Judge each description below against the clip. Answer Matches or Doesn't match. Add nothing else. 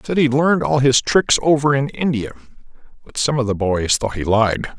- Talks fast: Matches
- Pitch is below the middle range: Matches